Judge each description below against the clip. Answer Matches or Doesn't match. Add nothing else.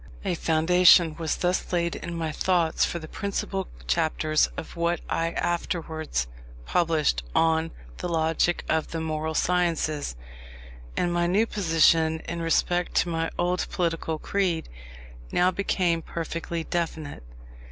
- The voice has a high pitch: Doesn't match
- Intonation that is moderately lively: Doesn't match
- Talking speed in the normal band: Doesn't match